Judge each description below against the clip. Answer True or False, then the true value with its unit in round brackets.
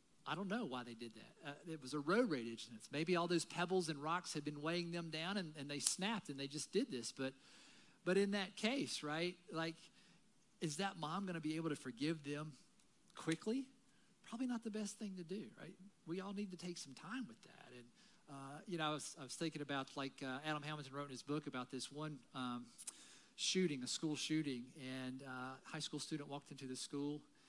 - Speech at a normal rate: False (225 wpm)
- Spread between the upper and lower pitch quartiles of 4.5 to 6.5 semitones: True (5.6 semitones)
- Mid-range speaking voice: True (155 Hz)